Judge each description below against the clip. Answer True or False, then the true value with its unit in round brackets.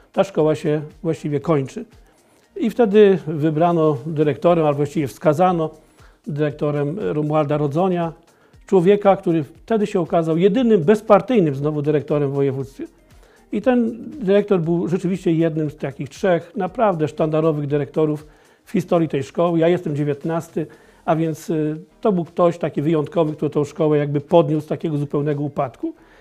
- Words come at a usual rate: True (140 wpm)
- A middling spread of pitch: True (3.7 semitones)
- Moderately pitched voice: True (160 Hz)